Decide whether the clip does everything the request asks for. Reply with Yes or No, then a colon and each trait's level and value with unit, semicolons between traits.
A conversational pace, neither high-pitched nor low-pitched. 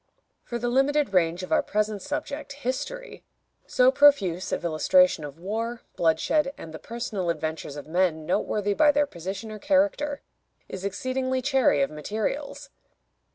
No: average, 150 wpm; high, 220 Hz